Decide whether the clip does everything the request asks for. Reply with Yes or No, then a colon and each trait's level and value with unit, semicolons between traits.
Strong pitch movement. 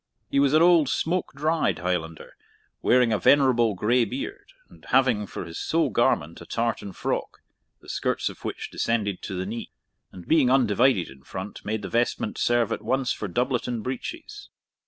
No: average, 4.9 semitones